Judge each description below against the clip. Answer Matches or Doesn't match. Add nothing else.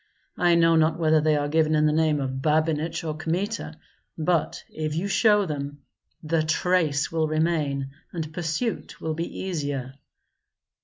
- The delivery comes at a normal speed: Matches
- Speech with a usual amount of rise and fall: Doesn't match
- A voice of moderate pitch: Matches